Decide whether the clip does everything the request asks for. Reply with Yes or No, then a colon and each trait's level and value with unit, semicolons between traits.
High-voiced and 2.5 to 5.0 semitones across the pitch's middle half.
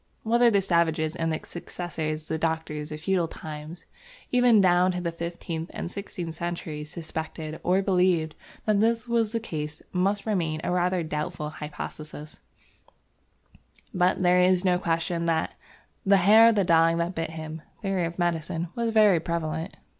No: medium, 170 Hz; average, 2.9 semitones